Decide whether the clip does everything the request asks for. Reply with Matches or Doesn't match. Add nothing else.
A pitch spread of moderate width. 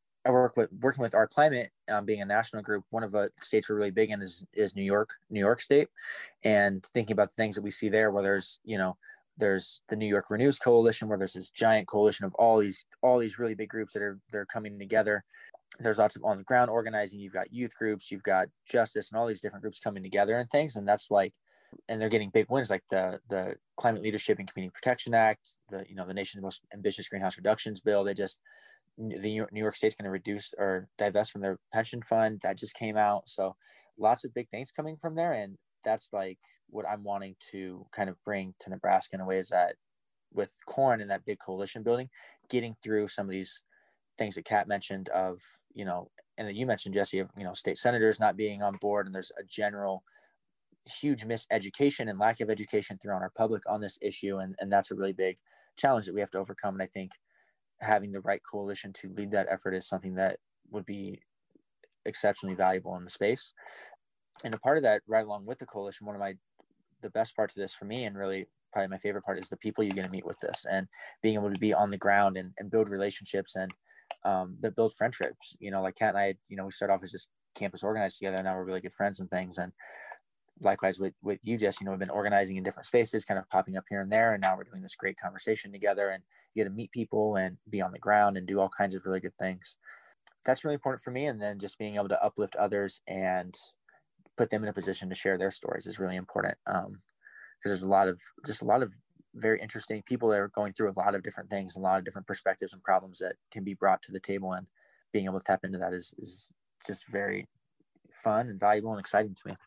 Doesn't match